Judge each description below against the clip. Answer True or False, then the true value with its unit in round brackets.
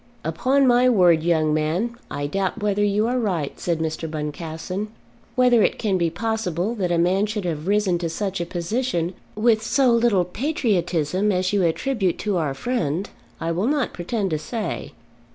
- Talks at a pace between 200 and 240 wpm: False (175 wpm)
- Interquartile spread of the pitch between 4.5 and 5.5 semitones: True (4.9 semitones)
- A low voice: False (190 Hz)